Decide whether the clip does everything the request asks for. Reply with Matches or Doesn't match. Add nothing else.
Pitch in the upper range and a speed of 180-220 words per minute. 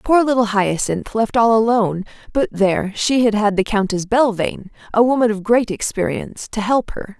Matches